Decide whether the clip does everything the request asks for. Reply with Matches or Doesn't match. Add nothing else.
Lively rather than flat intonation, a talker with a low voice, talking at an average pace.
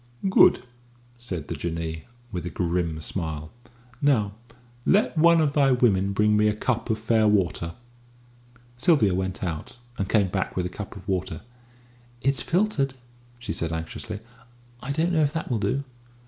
Matches